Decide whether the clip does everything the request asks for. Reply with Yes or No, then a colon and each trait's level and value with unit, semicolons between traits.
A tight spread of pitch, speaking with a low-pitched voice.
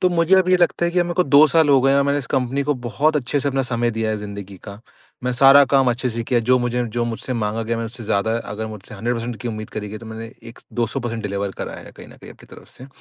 No: average, 3.9 semitones; low, 120 Hz